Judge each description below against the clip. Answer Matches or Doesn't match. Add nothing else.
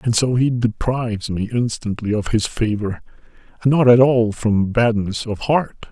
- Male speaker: Matches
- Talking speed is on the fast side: Doesn't match